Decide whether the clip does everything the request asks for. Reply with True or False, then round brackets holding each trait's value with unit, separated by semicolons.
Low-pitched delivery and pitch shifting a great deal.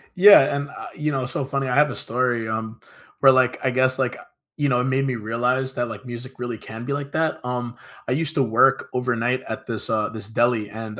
False (125 Hz; 2.7 semitones)